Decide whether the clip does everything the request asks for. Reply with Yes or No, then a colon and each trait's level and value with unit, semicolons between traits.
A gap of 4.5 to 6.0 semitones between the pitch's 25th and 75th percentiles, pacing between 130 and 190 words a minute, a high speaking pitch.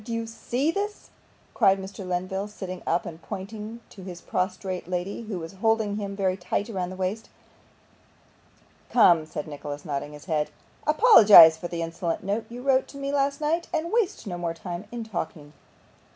Yes: average, 4.8 semitones; average, 180 wpm; high, 195 Hz